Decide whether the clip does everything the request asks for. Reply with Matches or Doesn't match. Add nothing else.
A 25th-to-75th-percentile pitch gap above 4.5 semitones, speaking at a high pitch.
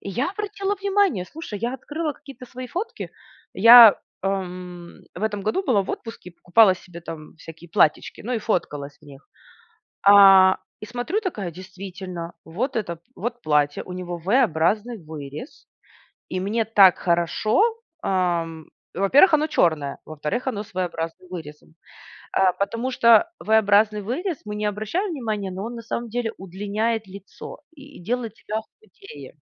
Matches